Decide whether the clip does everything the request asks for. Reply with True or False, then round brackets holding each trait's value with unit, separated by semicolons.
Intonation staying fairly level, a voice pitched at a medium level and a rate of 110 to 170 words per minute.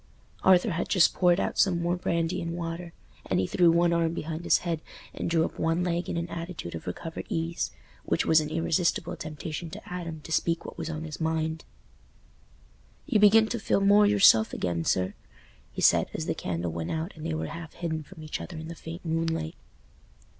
False (1.6 semitones; 165 Hz; 205 wpm)